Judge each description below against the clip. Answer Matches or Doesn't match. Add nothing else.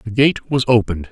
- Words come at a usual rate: Doesn't match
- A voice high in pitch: Doesn't match